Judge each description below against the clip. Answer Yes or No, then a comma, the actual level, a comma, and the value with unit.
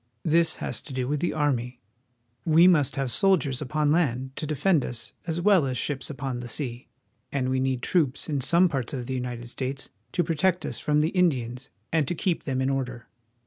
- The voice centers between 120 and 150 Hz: Yes, medium, 140 Hz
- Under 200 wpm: No, fast, 205 wpm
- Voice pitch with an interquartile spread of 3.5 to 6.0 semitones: Yes, average, 4.0 semitones